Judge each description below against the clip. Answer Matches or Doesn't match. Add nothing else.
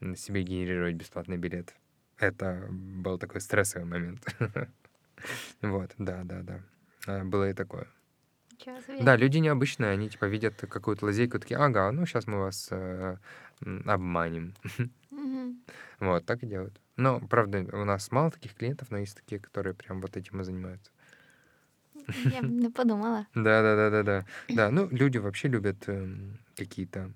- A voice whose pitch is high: Doesn't match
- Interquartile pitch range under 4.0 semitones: Doesn't match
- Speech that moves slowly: Doesn't match